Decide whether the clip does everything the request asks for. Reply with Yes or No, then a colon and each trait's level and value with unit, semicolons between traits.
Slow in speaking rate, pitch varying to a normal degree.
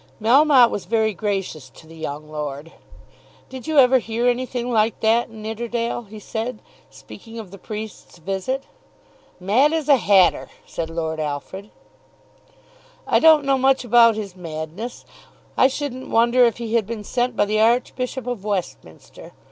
No: average, 155 wpm; average, 4.6 semitones